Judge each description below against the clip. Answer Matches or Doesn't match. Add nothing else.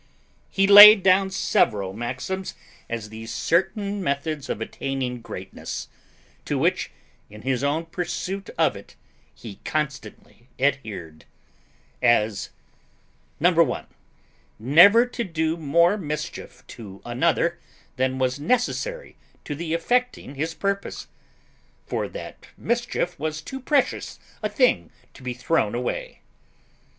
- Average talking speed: Doesn't match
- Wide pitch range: Matches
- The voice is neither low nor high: Matches